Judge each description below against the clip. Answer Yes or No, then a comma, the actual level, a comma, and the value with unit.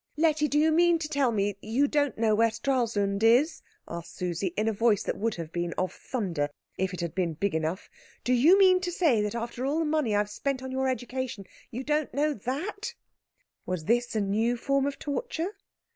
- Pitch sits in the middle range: No, high, 240 Hz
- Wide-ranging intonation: Yes, wide, 6.3 semitones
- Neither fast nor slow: No, fast, 220 wpm